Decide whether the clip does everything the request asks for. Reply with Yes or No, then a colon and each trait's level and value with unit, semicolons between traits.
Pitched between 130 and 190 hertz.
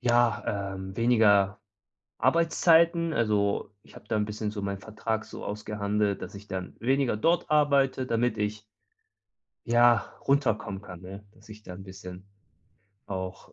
No: low, 105 Hz